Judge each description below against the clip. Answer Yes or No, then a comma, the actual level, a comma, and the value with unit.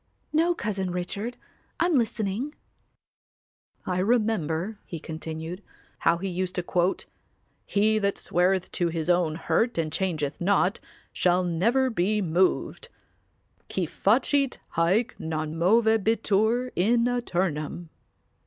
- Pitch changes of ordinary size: Yes, average, 4.5 semitones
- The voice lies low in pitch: No, high, 190 Hz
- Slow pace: Yes, slow, 115 wpm